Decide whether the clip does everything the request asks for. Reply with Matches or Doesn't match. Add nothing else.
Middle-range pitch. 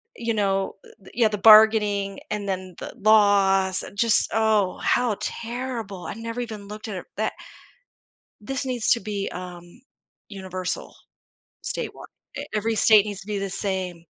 Doesn't match